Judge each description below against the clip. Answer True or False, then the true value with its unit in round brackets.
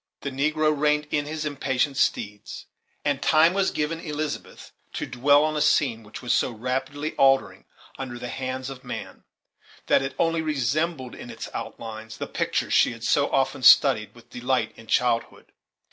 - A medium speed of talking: True (170 wpm)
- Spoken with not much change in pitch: False (3.5 semitones)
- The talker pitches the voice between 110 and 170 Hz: True (135 Hz)